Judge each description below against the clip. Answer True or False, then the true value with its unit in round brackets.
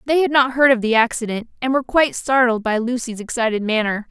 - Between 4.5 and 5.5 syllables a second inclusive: False (6.3 syllables/s)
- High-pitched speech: True (240 Hz)